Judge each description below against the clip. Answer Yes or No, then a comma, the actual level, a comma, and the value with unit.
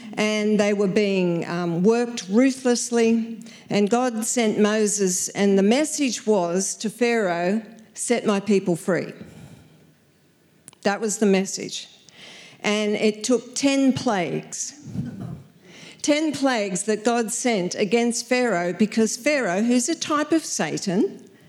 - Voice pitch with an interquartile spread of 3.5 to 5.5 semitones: No, average, 3.0 semitones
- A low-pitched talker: No, high, 220 Hz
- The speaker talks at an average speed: No, slow, 125 wpm